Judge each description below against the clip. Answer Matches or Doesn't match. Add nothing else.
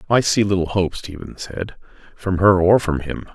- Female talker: Doesn't match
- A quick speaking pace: Doesn't match